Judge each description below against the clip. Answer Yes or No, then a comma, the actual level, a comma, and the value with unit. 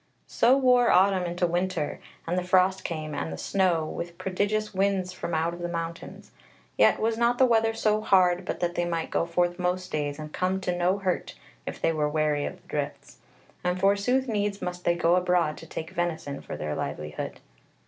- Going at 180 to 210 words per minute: Yes, average, 200 wpm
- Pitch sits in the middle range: Yes, medium, 180 Hz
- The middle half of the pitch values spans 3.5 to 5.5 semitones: No, average, 2.7 semitones